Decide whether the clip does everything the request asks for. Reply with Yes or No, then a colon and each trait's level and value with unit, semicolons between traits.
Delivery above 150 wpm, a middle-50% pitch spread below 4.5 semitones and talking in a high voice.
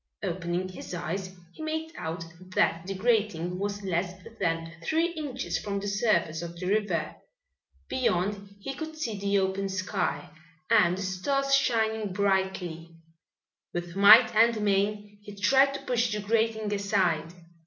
No: average, 145 wpm; average, 3.4 semitones; high, 200 Hz